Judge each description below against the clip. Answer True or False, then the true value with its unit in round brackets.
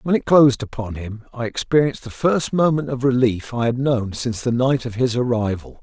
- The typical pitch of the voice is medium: False (125 Hz)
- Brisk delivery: True (215 wpm)